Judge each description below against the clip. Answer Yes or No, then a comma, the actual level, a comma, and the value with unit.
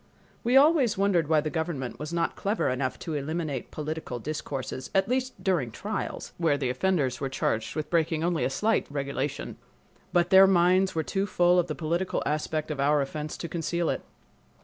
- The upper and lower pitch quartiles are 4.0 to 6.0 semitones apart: Yes, average, 4.3 semitones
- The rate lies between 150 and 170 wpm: No, average, 180 wpm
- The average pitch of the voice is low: No, medium, 160 Hz